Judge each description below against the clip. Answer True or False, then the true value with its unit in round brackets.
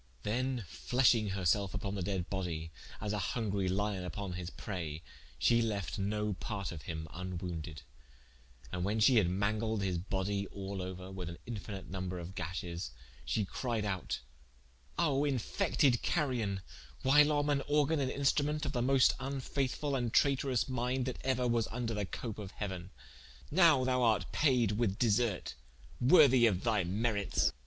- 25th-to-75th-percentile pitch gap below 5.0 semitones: False (5.3 semitones)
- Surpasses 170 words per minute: False (160 wpm)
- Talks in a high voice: False (105 Hz)